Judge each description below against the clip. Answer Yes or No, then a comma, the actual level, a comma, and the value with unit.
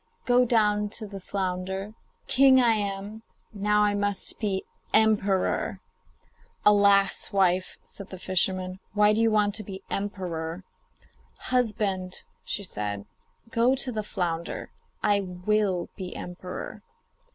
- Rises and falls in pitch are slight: Yes, narrow, 2.3 semitones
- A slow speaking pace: Yes, slow, 125 wpm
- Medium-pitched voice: No, high, 200 Hz